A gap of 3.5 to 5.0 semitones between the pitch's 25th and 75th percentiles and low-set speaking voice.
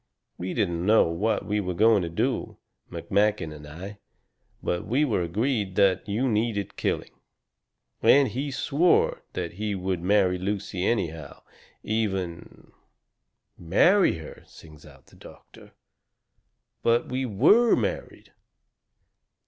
Yes: average, 4.4 semitones; low, 100 Hz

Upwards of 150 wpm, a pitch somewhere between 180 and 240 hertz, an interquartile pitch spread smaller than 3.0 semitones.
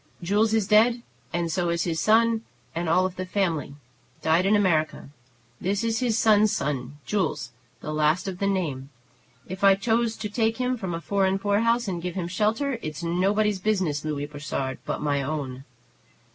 No: average, 175 wpm; medium, 185 Hz; wide, 5.4 semitones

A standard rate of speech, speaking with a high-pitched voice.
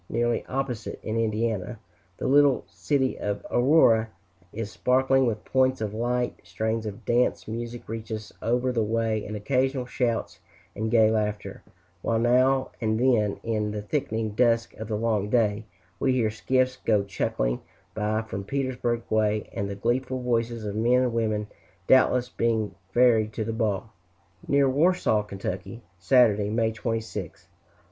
No: average, 155 wpm; low, 115 Hz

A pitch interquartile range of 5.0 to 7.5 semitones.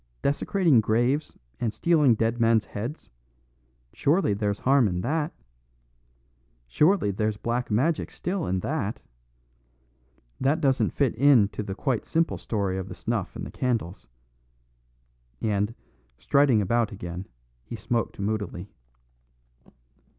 Yes: wide, 5.5 semitones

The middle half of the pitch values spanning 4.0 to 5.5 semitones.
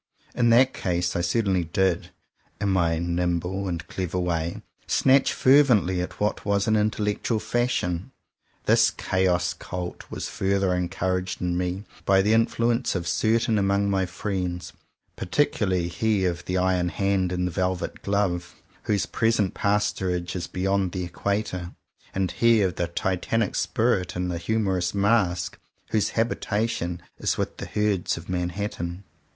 No: average, 2.8 semitones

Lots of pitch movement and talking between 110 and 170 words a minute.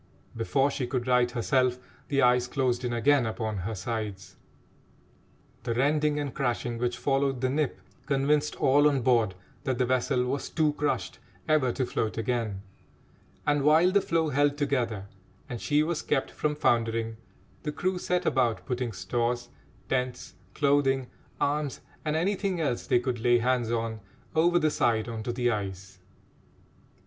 No: average, 3.8 semitones; average, 155 wpm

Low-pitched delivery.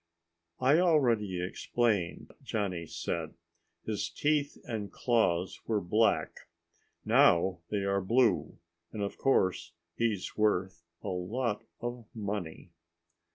Yes: low, 105 Hz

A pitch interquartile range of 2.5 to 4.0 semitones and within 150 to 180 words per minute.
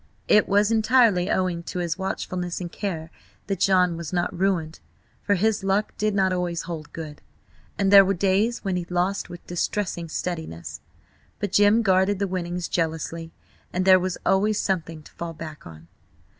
Yes: average, 2.8 semitones; average, 170 wpm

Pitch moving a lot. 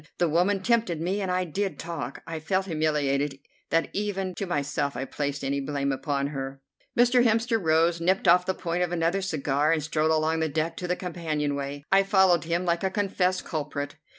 No: average, 4.2 semitones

